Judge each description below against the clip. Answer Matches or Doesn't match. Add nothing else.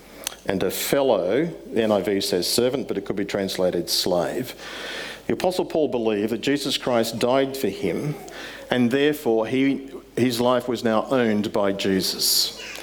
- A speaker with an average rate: Matches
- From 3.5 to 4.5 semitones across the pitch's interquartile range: Matches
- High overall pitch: Doesn't match